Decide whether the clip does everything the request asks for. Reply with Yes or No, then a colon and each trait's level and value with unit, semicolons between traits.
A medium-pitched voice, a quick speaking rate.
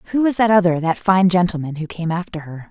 Yes: medium, 180 Hz; fast, 245 wpm